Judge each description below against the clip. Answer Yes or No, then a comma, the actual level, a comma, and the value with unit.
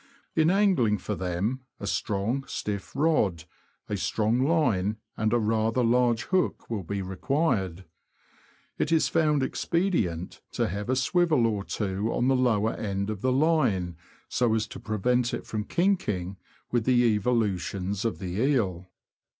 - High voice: No, low, 110 Hz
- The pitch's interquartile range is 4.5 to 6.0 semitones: Yes, average, 4.9 semitones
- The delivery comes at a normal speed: Yes, average, 160 wpm